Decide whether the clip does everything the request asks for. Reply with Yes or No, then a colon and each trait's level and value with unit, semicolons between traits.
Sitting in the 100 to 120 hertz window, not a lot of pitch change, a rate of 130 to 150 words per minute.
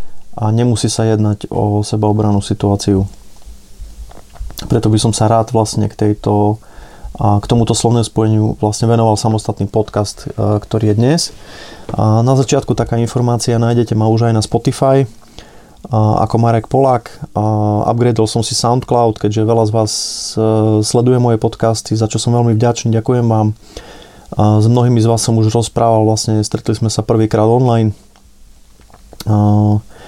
Yes: low, 110 Hz; narrow, 1.6 semitones; average, 140 wpm